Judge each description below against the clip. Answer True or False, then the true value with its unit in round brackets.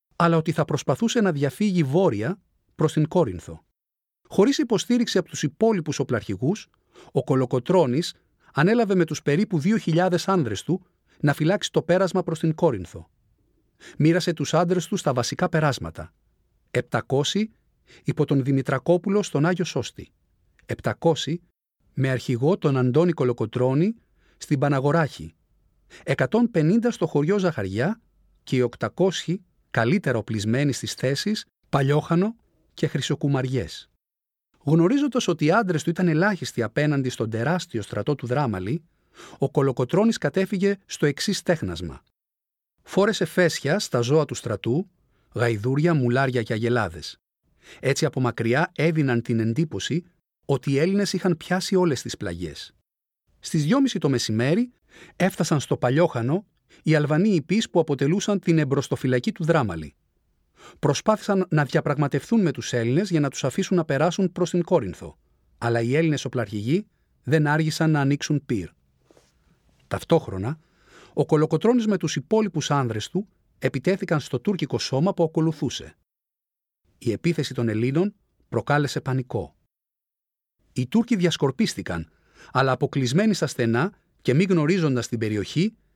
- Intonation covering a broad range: True (6.3 semitones)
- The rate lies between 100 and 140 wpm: True (125 wpm)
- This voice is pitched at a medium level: True (150 Hz)